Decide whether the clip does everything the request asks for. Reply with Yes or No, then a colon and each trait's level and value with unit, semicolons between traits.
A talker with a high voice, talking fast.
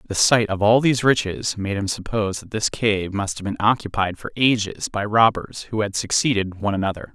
No: low, 105 Hz; fast, 210 wpm